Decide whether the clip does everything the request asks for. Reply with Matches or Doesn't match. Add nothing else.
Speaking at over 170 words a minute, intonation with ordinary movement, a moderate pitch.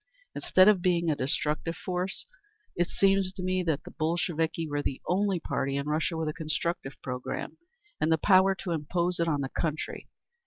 Matches